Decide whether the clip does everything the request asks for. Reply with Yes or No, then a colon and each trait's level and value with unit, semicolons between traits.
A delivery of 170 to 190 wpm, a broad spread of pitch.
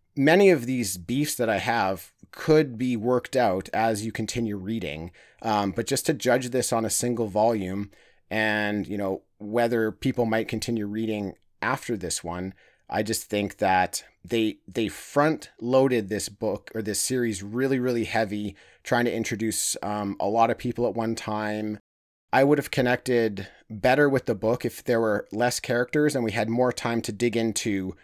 No: average, 180 wpm; average, 2.9 semitones